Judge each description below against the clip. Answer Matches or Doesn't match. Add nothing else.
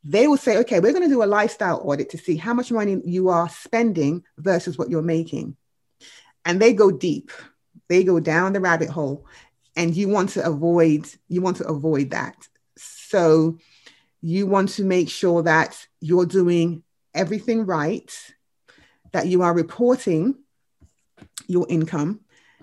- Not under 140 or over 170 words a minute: Matches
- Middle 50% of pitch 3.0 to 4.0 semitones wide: Matches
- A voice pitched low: Doesn't match